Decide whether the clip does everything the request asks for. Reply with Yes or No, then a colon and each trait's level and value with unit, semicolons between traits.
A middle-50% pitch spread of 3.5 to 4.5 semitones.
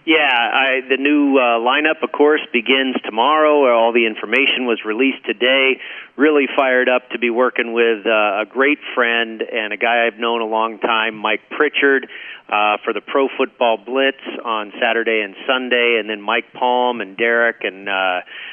No: average, 2.8 semitones